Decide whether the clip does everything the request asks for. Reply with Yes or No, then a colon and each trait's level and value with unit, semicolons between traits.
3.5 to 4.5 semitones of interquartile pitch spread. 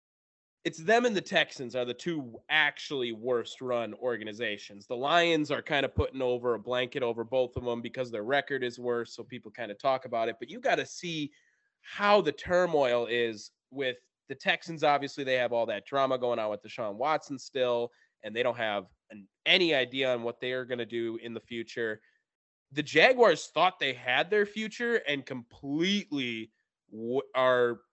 Yes: average, 3.9 semitones